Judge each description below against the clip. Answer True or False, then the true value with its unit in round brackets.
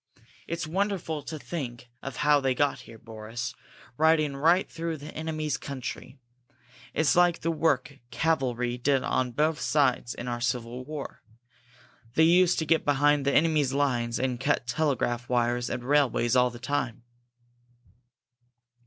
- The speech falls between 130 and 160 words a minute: True (145 wpm)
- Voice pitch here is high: False (140 Hz)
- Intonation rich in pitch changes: False (4.3 semitones)